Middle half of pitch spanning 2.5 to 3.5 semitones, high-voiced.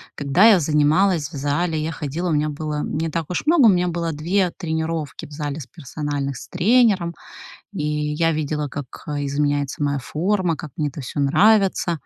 No: average, 3.1 semitones; medium, 155 Hz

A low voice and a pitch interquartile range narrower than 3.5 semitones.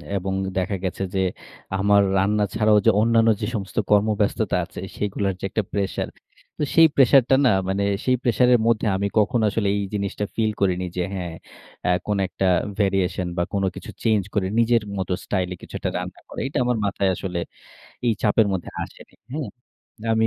Yes: low, 105 Hz; average, 2.7 semitones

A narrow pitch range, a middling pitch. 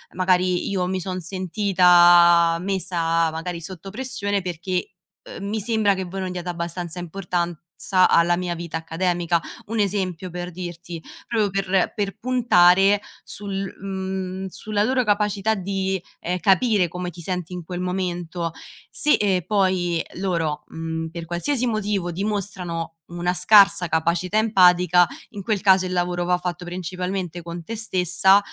Yes: narrow, 2.1 semitones; medium, 180 Hz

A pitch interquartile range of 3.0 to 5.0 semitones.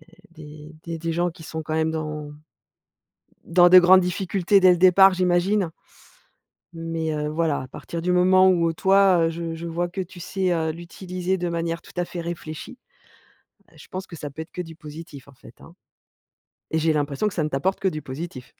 No: narrow, 2.4 semitones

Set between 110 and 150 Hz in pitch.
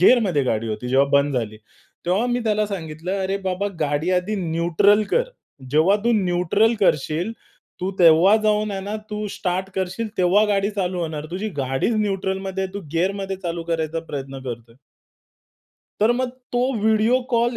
No: medium, 185 Hz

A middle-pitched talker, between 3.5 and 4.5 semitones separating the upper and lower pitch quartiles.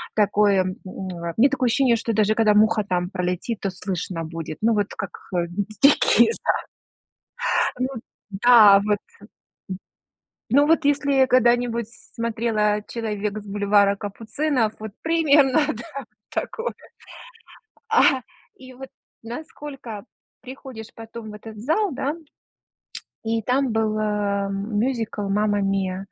No: high, 220 Hz; average, 4.0 semitones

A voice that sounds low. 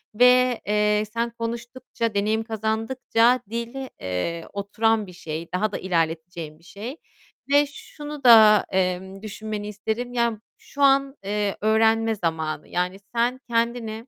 No: high, 220 Hz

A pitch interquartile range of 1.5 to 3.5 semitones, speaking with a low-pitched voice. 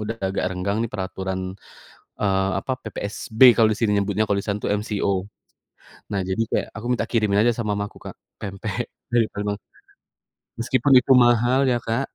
Yes: narrow, 2.6 semitones; low, 105 Hz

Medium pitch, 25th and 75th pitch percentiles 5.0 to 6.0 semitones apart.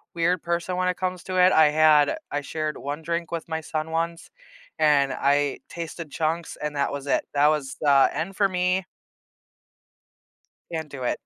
No: medium, 160 Hz; average, 2.8 semitones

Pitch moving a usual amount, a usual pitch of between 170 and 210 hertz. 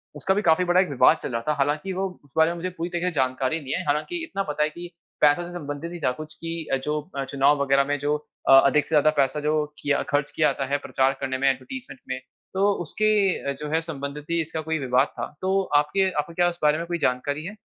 No: average, 3.7 semitones; medium, 150 Hz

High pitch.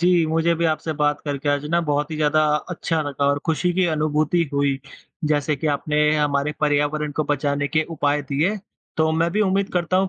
No: medium, 150 Hz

